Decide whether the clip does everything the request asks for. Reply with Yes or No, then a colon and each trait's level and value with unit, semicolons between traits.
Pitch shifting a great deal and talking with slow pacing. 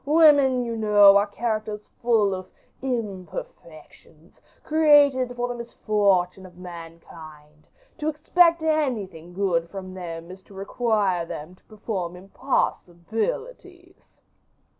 Yes: wide, 5.8 semitones; slow, 110 wpm